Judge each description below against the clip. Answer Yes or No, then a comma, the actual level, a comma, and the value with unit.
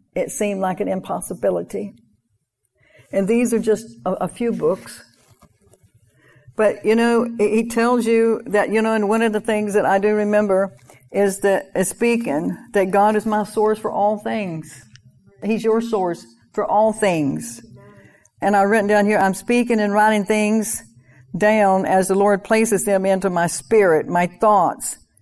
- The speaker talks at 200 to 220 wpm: No, average, 165 wpm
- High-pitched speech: Yes, high, 205 Hz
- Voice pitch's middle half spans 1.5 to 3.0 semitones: No, average, 4.3 semitones